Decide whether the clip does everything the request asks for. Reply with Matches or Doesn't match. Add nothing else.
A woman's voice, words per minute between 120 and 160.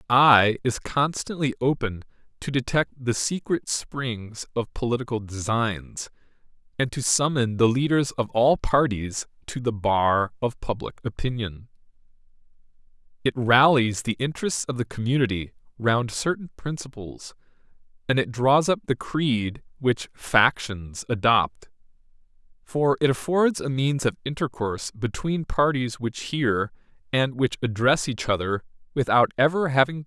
Doesn't match